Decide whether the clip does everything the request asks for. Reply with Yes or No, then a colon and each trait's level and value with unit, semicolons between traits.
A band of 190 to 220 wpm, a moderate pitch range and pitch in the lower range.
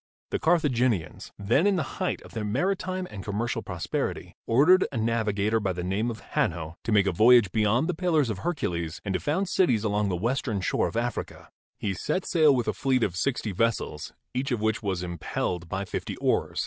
No: average, 200 wpm; wide, 5.8 semitones; low, 110 Hz